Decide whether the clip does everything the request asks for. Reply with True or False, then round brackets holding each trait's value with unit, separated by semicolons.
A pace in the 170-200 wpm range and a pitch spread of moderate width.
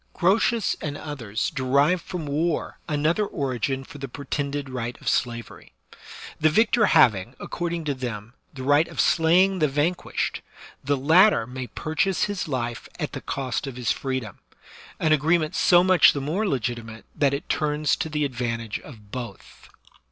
False (160 wpm; 4.4 semitones)